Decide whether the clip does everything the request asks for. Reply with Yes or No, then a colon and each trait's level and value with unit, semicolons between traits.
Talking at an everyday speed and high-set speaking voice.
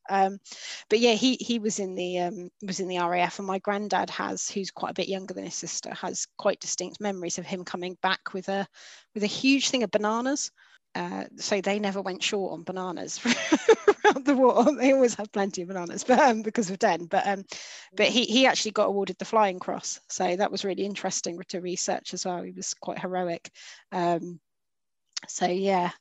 No: fast, 210 wpm; high, 195 Hz